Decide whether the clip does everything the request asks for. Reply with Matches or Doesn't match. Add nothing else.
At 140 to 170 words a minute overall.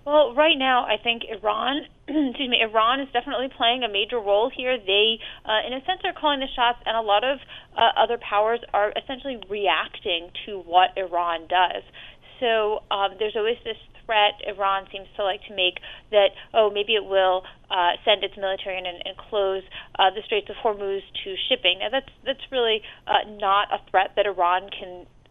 Doesn't match